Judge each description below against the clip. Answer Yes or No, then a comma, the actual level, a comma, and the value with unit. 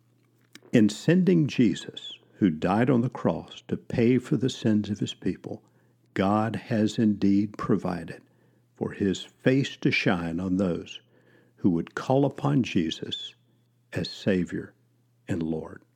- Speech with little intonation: No, average, 4.4 semitones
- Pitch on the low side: Yes, low, 115 Hz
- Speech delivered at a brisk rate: No, slow, 135 wpm